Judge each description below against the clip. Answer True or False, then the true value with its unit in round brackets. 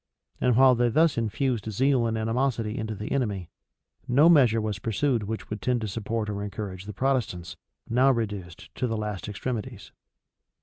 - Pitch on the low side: True (110 Hz)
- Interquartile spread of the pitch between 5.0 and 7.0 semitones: False (3.4 semitones)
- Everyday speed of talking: True (175 wpm)